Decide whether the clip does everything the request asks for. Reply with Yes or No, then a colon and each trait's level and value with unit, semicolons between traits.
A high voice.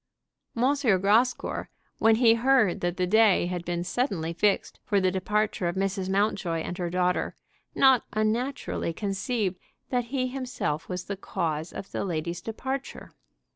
Yes: high, 200 Hz